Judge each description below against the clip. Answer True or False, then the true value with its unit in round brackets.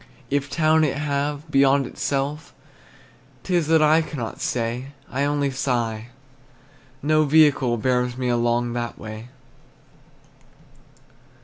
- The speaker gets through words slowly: True (115 wpm)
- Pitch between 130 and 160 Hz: True (140 Hz)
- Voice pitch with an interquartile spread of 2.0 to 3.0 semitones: False (3.6 semitones)